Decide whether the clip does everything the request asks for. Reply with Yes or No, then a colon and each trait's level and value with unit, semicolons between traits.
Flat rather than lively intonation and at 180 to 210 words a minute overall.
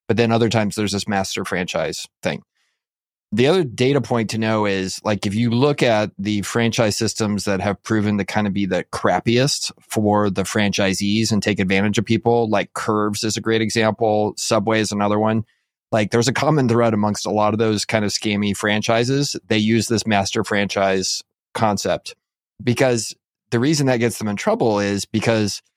Yes: narrow, 2.1 semitones; average, 190 wpm